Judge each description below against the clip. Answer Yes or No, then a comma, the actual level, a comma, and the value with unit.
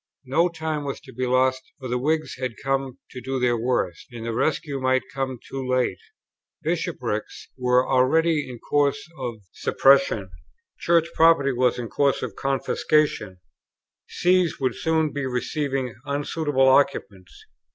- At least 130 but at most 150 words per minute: Yes, average, 145 wpm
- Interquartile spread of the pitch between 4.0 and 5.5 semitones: No, average, 2.8 semitones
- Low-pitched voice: Yes, low, 130 Hz